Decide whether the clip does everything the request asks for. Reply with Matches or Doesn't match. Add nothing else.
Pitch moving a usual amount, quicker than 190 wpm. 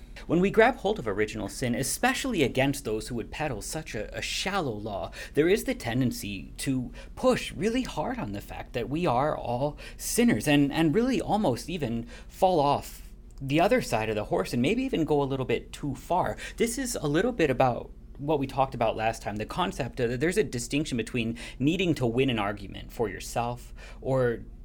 Doesn't match